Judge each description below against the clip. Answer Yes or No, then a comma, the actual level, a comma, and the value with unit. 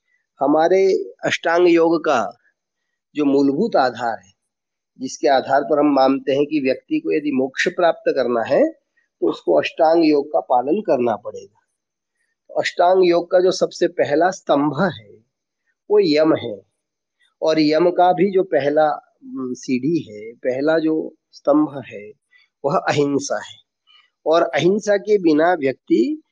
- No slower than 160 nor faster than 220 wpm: No, average, 140 wpm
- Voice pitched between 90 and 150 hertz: No, medium, 175 Hz